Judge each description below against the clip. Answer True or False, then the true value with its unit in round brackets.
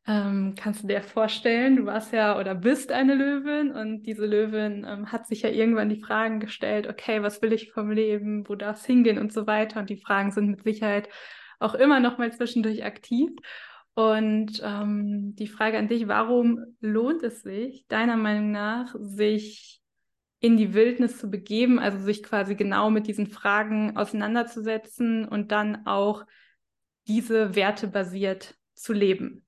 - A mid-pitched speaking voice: False (220 Hz)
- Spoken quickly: False (165 wpm)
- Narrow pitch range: True (1.7 semitones)